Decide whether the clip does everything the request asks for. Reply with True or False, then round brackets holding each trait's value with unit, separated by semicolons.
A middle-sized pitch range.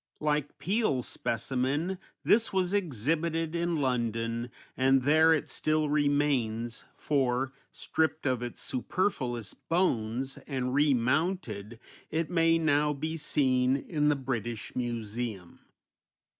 True (4.5 semitones)